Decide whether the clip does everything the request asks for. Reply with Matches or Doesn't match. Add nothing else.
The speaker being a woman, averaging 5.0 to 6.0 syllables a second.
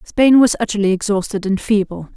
Matches